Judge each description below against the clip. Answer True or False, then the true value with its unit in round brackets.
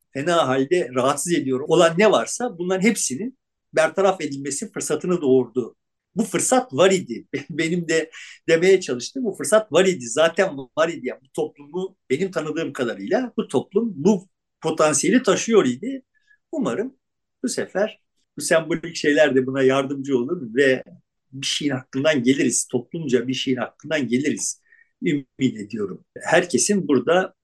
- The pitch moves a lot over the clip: True (6.3 semitones)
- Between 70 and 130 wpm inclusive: False (140 wpm)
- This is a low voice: False (165 Hz)